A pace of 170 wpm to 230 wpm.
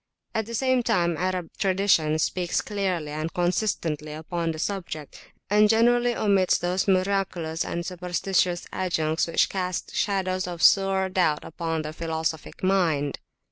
No: average, 140 wpm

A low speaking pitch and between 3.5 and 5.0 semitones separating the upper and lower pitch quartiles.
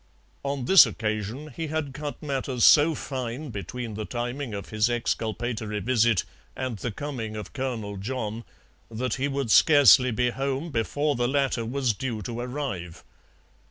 Yes: low, 125 Hz; average, 3.9 semitones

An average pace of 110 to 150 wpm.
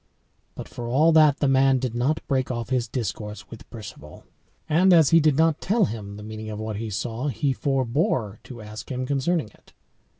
No: average, 200 wpm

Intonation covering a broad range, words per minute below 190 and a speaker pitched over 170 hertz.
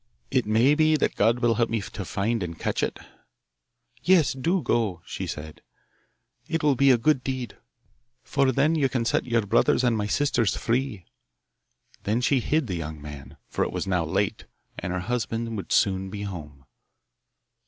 No: wide, 5.7 semitones; average, 180 wpm; low, 115 Hz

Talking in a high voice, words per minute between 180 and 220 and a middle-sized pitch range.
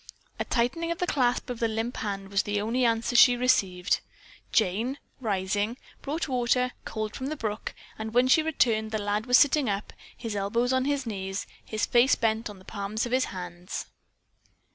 Yes: high, 225 Hz; average, 185 wpm; average, 3.6 semitones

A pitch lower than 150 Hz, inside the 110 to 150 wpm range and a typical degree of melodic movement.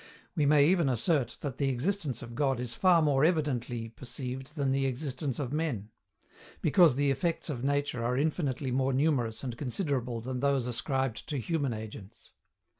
No: low, 135 Hz; average, 170 wpm; average, 3.3 semitones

